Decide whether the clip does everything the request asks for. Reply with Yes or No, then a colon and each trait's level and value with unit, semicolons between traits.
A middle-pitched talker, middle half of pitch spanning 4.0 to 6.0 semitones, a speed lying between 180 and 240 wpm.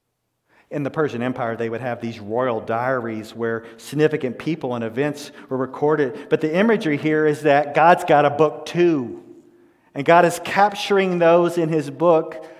No: medium, 150 Hz; average, 4.9 semitones; average, 170 wpm